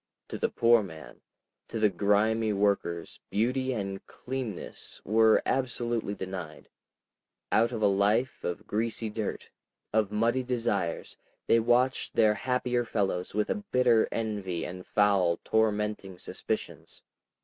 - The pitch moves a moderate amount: Yes, average, 3.0 semitones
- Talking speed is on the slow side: Yes, slow, 125 wpm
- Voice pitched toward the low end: Yes, low, 110 Hz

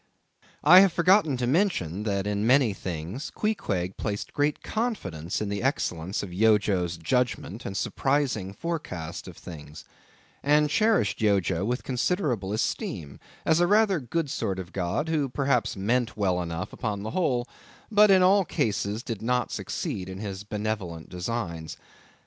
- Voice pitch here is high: No, low, 110 Hz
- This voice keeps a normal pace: Yes, average, 150 wpm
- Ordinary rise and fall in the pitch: No, wide, 7.7 semitones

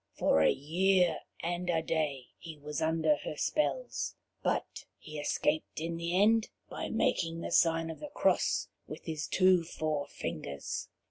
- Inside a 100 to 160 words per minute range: Yes, average, 150 wpm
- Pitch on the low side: No, medium, 165 Hz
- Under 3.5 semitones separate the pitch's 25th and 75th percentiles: Yes, narrow, 2.4 semitones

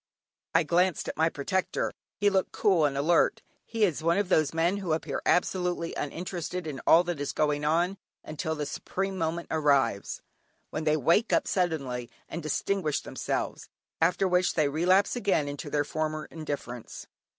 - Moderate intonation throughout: Yes, average, 3.4 semitones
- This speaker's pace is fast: No, average, 165 wpm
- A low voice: No, medium, 165 Hz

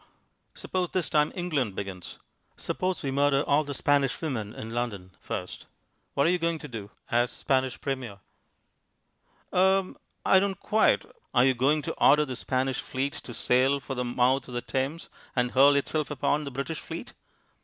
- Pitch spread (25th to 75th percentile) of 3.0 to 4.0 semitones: Yes, average, 3.5 semitones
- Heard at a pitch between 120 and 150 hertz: Yes, low, 135 Hz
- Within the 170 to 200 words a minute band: Yes, average, 175 wpm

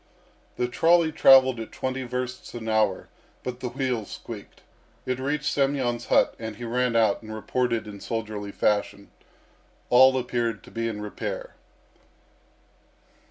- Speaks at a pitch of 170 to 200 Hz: No, low, 120 Hz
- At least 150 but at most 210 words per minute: No, average, 140 wpm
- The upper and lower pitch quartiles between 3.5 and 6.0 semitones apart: No, average, 3.1 semitones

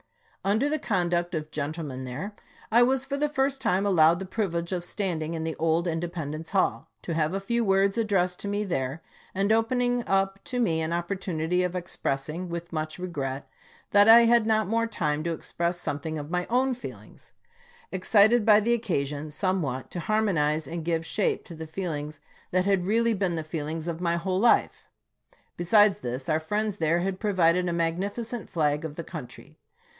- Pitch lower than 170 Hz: No, medium, 180 Hz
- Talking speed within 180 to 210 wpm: Yes, average, 190 wpm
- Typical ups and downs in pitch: Yes, average, 4.4 semitones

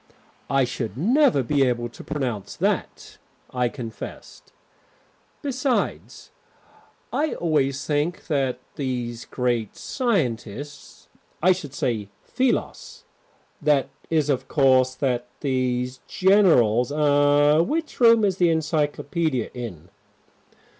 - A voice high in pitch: No, medium, 140 Hz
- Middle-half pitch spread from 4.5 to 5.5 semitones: Yes, average, 5.2 semitones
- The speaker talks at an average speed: No, slow, 105 wpm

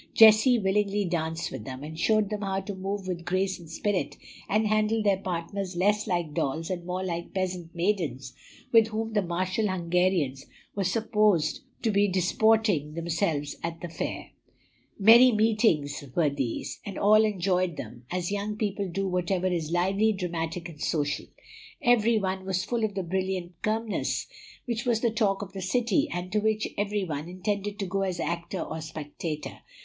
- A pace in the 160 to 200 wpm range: Yes, average, 175 wpm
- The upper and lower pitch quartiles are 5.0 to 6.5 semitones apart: No, average, 3.7 semitones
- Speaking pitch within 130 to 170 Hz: No, high, 190 Hz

